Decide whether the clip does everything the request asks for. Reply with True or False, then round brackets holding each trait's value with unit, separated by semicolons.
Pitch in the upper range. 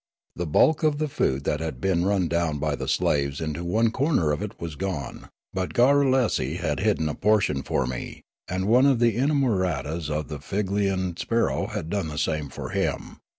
False (90 Hz)